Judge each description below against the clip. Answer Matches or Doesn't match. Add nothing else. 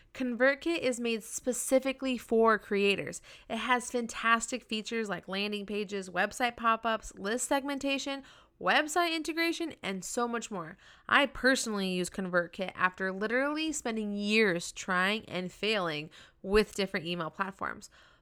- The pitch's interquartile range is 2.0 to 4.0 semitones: Doesn't match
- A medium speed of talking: Doesn't match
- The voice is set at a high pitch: Matches